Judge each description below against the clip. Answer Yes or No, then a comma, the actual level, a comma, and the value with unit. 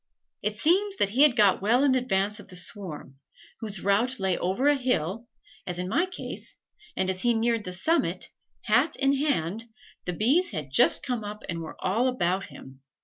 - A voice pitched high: Yes, high, 210 Hz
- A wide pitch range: Yes, wide, 5.7 semitones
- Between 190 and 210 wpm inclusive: Yes, average, 195 wpm